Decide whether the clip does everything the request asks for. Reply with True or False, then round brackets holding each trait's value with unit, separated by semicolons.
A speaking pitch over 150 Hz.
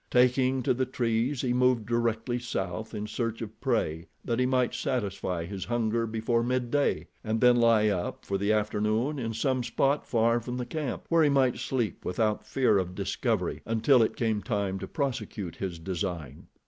False (115 Hz)